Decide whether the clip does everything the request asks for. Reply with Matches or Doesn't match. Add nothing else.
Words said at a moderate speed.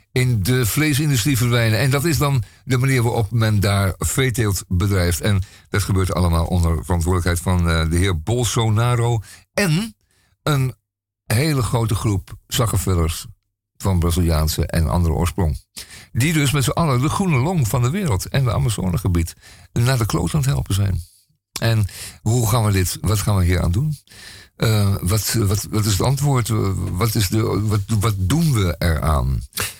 Matches